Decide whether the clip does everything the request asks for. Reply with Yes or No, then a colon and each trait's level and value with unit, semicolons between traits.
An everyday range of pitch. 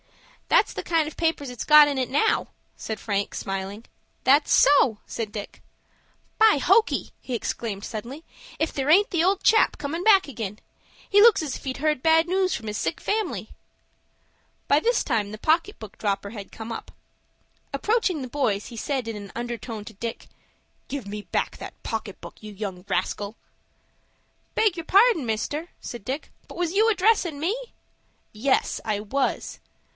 No: wide, 7.6 semitones